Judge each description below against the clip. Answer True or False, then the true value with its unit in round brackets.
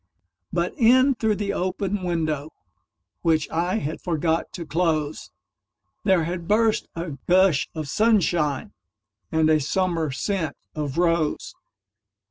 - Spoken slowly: True (105 wpm)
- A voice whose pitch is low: False (170 Hz)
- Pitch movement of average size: True (3.5 semitones)